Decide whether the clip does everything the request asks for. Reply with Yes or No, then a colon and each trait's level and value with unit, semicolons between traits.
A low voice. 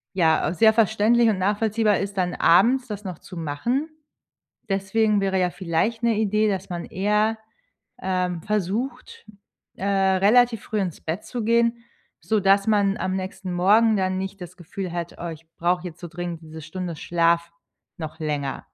No: high, 190 Hz